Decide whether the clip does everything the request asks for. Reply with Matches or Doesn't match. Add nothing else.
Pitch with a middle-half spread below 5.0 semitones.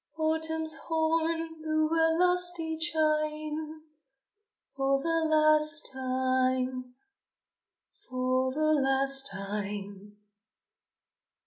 Matches